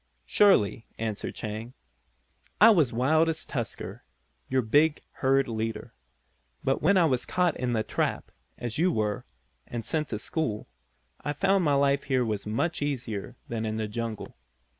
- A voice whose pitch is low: Yes, low, 130 Hz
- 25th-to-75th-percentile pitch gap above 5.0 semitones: Yes, wide, 5.6 semitones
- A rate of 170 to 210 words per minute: No, average, 160 wpm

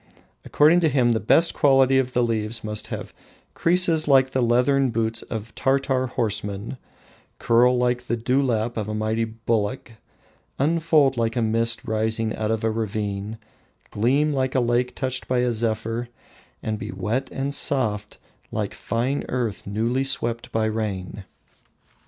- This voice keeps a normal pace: Yes, average, 150 wpm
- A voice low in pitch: Yes, low, 120 Hz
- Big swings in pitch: No, average, 3.1 semitones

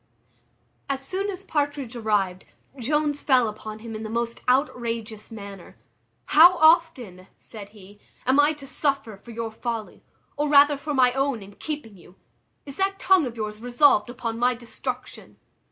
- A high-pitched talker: Yes, high, 245 Hz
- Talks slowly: No, average, 160 wpm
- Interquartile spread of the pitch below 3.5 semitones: No, average, 5.0 semitones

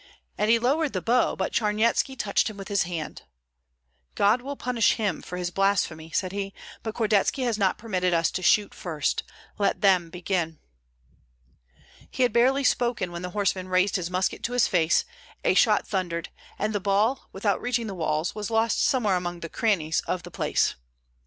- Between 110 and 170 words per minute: No, average, 185 wpm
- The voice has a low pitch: No, high, 200 Hz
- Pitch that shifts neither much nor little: Yes, average, 4.1 semitones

